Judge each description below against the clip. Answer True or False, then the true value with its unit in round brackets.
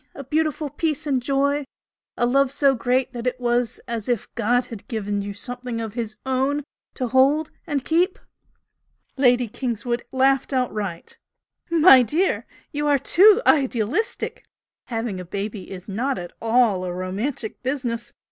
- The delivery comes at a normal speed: True (155 wpm)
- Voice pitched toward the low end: False (250 Hz)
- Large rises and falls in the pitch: False (3.7 semitones)